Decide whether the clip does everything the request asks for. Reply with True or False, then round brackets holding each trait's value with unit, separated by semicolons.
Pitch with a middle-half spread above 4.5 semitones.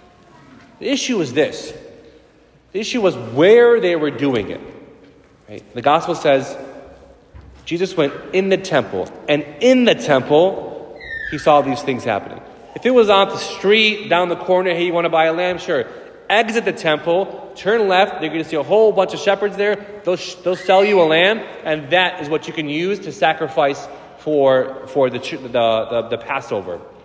True (5.5 semitones)